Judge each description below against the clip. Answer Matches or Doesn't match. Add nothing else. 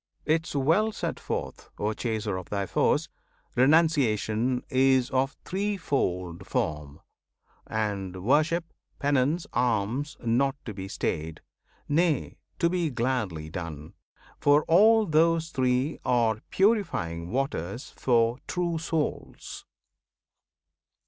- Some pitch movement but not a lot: Doesn't match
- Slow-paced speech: Matches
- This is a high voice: Doesn't match